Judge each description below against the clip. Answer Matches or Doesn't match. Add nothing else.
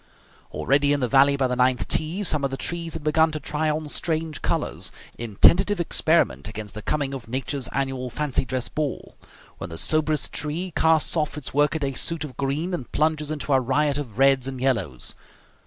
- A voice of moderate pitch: Matches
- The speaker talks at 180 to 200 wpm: Matches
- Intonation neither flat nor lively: Matches